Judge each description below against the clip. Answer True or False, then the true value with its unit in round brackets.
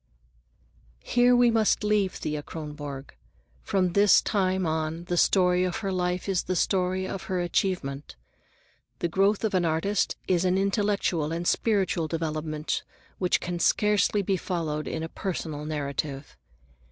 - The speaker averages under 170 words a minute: True (145 wpm)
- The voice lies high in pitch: False (180 Hz)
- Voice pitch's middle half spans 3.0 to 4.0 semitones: True (3.6 semitones)